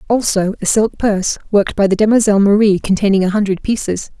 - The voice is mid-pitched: No, high, 205 Hz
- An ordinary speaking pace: Yes, average, 185 wpm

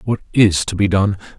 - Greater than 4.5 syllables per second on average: Yes, 5.2 syllables/s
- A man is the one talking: Yes, male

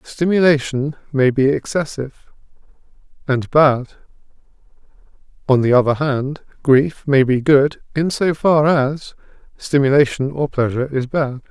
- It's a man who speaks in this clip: Yes, male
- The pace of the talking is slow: Yes, slow, 120 wpm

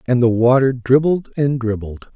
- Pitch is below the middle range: Yes, low, 125 Hz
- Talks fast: No, average, 165 wpm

